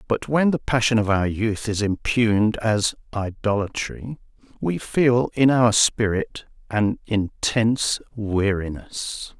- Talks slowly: Yes, slow, 120 wpm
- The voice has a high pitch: No, low, 110 Hz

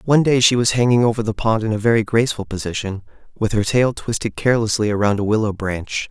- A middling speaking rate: No, fast, 215 wpm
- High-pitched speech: No, low, 110 Hz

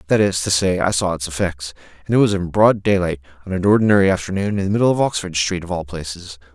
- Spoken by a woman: No, male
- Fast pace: Yes, fast, 245 wpm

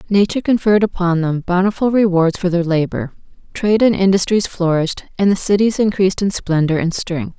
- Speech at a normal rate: Yes, average, 170 wpm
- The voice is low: No, medium, 185 Hz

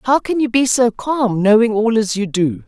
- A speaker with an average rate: No, fast, 245 wpm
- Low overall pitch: No, high, 230 Hz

